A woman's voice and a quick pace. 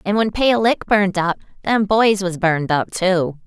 Yes: female; fast, 210 wpm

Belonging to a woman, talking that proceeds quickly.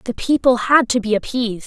Yes: female; fast, 215 wpm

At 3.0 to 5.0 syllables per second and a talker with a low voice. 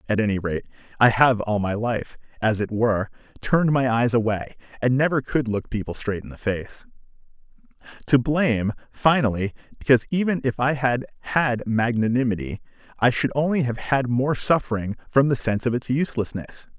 No: 5.6 syllables/s; low, 120 Hz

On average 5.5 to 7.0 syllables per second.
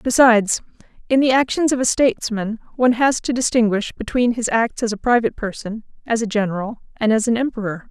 Yes: 6.0 syllables/s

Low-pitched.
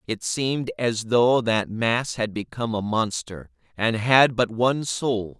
Yes: low, 115 Hz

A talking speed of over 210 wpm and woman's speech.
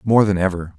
No: fast, 230 wpm; male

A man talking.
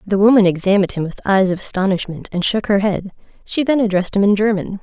No: female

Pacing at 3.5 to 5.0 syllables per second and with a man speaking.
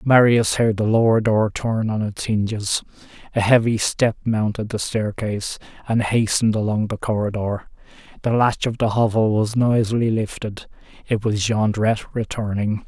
Yes: 4.8 syllables/s; male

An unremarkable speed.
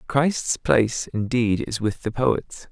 Yes: average, 155 wpm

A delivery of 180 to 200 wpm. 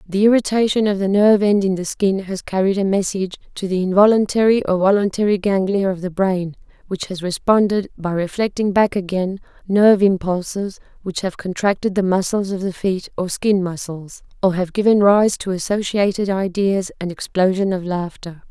No: average, 170 wpm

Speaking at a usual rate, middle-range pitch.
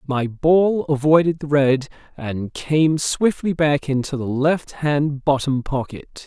Yes: average, 145 wpm; medium, 145 Hz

